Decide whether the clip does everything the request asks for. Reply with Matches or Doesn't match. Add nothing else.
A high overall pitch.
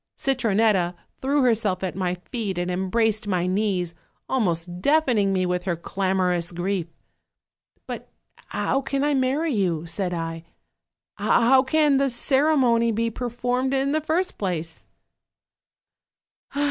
Matches